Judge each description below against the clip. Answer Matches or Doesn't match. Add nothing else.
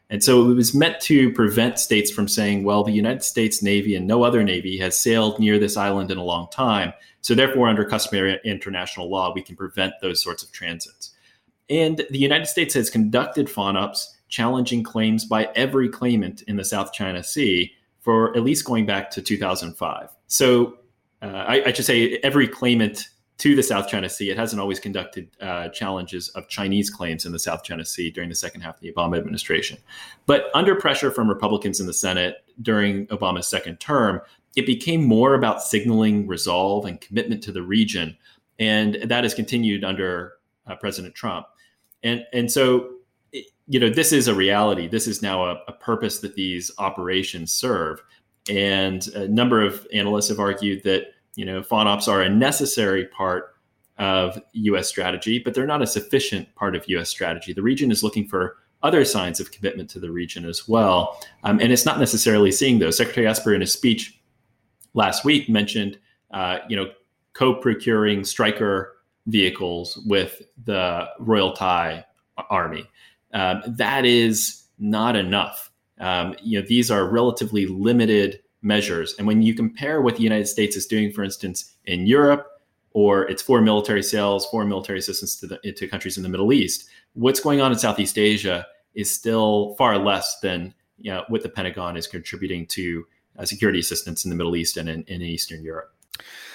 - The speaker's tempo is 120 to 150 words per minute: Doesn't match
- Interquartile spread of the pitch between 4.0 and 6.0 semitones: Doesn't match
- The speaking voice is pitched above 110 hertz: Doesn't match